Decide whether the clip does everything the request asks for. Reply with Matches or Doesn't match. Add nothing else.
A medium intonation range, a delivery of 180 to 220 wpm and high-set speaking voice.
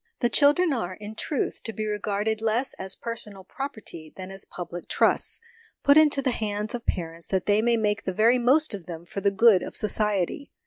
Matches